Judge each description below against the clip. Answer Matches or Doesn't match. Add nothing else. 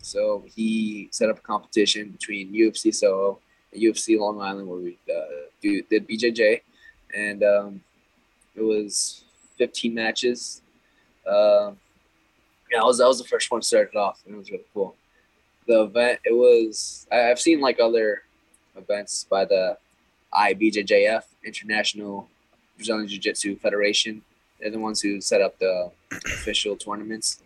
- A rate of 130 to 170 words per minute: Matches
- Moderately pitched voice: Doesn't match